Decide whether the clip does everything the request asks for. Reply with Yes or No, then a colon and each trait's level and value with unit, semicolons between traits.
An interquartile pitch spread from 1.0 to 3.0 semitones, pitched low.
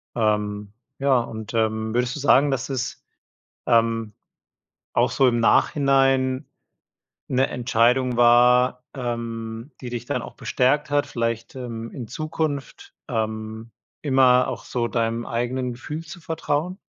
Yes: narrow, 2.6 semitones; low, 125 Hz